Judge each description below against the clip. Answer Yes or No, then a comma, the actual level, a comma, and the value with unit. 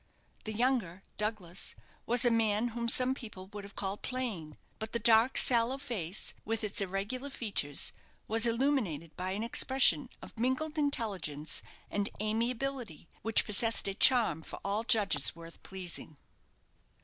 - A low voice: No, high, 220 Hz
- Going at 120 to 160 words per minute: Yes, average, 145 wpm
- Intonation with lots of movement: No, average, 4.0 semitones